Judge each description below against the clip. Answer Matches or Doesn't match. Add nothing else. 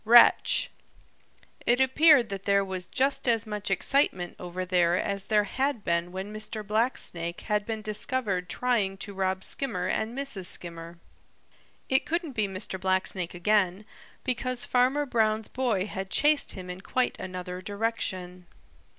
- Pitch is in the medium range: Doesn't match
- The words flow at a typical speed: Matches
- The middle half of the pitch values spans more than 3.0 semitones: Matches